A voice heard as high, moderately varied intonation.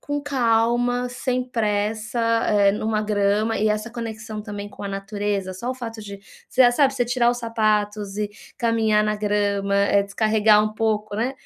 No: high, 215 Hz; narrow, 2.3 semitones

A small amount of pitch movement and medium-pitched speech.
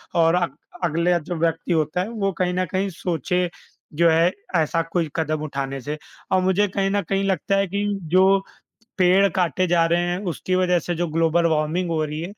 Yes: narrow, 2.3 semitones; medium, 175 Hz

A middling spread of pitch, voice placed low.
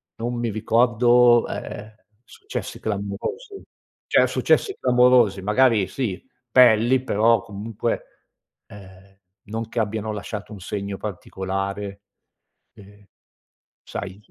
Yes: average, 3.0 semitones; low, 110 Hz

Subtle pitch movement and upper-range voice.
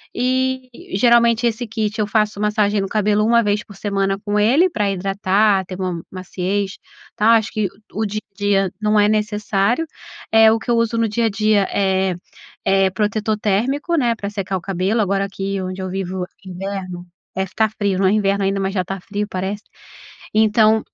Yes: narrow, 2.1 semitones; high, 205 Hz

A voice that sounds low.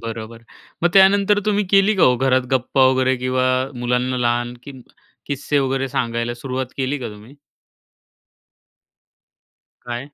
Yes: low, 130 Hz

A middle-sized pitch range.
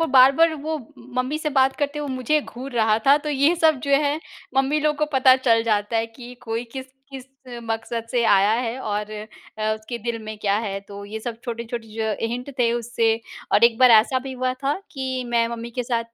Yes: average, 3.1 semitones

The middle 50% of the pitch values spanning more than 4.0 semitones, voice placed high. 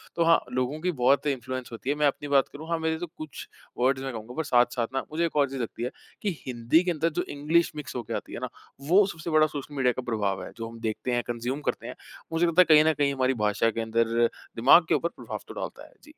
No: average, 4.5 semitones; low, 135 Hz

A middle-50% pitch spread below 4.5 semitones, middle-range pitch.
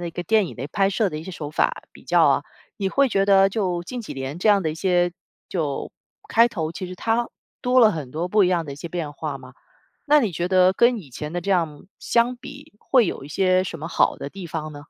No: average, 4.8 semitones; medium, 180 Hz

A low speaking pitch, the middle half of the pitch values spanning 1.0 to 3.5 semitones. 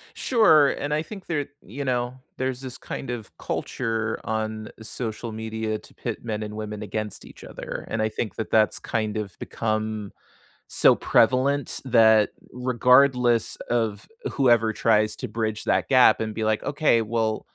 Yes: low, 110 Hz; average, 2.8 semitones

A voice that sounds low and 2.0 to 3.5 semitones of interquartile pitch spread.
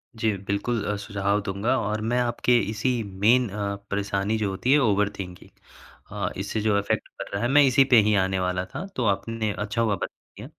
Yes: low, 105 Hz; narrow, 2.6 semitones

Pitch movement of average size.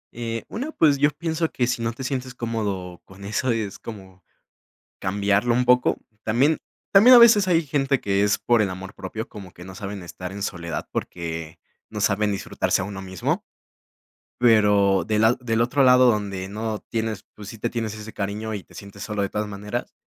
Yes: average, 3.9 semitones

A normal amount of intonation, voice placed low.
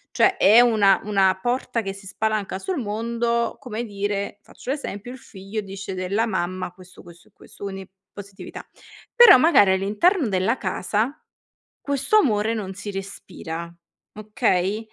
No: average, 3.5 semitones; high, 205 Hz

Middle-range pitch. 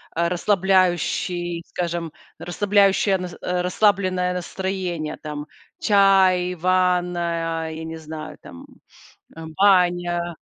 Yes: medium, 180 Hz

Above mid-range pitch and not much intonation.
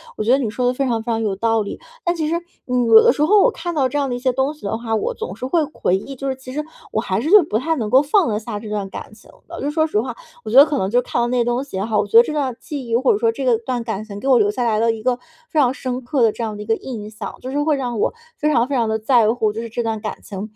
No: high, 240 Hz; average, 3.6 semitones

